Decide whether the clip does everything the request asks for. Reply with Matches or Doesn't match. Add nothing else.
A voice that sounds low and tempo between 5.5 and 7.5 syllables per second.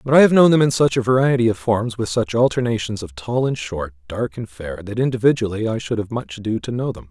Matches